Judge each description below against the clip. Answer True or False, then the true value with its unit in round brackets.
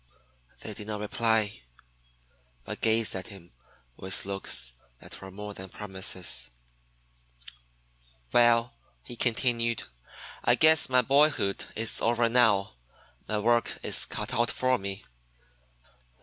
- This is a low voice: True (110 Hz)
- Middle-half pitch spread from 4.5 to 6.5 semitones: False (3.3 semitones)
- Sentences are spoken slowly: True (120 wpm)